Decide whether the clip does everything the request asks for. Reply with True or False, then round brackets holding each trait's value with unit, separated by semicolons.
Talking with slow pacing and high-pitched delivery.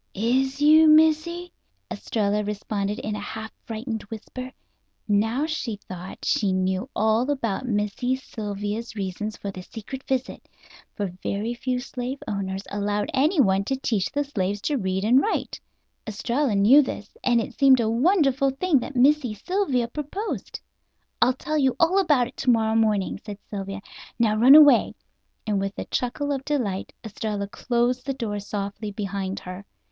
False (160 wpm; 230 Hz)